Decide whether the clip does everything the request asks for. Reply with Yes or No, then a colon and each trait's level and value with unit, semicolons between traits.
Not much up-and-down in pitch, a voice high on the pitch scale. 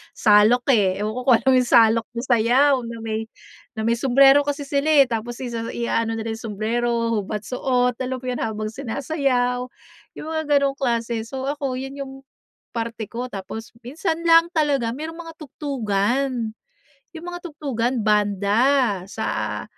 No: average, 3.7 semitones; high, 245 Hz